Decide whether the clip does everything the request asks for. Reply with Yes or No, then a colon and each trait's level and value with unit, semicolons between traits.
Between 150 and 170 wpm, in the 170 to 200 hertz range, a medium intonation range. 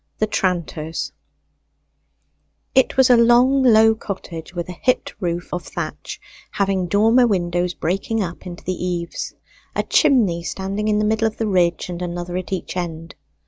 Yes: average, 160 wpm; medium, 185 Hz; average, 4.0 semitones